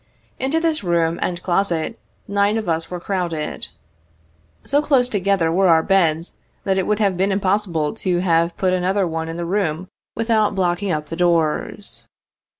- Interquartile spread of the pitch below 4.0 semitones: Yes, average, 3.3 semitones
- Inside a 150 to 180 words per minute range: Yes, average, 165 wpm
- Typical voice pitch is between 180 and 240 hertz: Yes, medium, 185 Hz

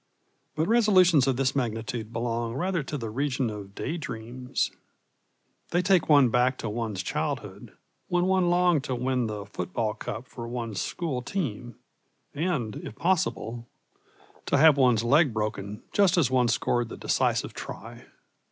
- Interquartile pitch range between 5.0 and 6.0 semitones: Yes, wide, 5.6 semitones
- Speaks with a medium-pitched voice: No, low, 125 Hz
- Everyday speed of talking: Yes, average, 150 wpm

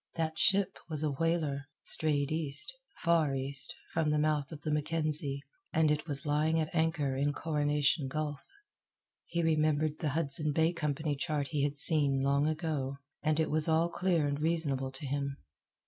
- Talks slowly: No, average, 170 wpm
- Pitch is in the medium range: Yes, medium, 150 Hz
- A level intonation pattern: Yes, narrow, 2.1 semitones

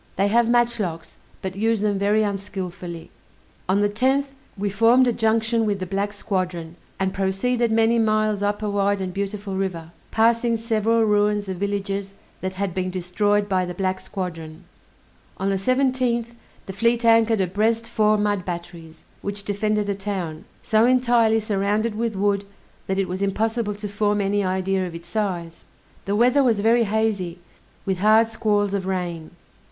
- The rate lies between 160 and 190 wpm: Yes, average, 170 wpm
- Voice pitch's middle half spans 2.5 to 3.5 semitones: Yes, average, 2.8 semitones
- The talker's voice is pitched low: No, high, 205 Hz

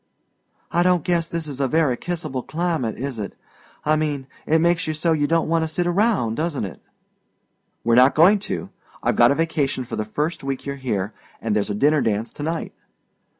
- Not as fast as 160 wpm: No, fast, 205 wpm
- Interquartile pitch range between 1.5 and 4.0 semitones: No, average, 4.7 semitones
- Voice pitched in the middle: Yes, medium, 150 Hz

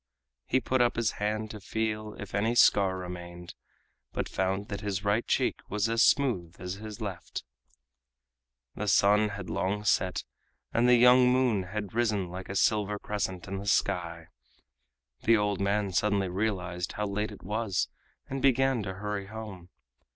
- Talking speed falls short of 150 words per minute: No, average, 165 wpm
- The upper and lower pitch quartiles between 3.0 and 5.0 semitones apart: No, narrow, 2.6 semitones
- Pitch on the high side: No, low, 105 Hz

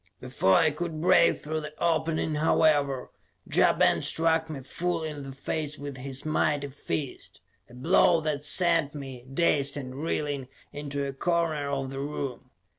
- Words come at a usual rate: Yes, average, 160 wpm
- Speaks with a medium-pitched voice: Yes, medium, 150 Hz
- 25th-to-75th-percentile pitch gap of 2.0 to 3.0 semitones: Yes, narrow, 2.6 semitones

